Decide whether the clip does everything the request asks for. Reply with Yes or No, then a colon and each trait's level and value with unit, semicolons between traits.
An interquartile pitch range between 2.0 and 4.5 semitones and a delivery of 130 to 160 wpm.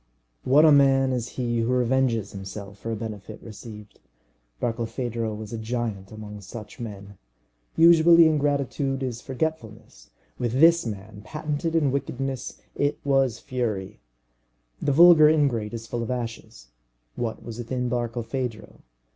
Yes: average, 3.8 semitones; slow, 135 wpm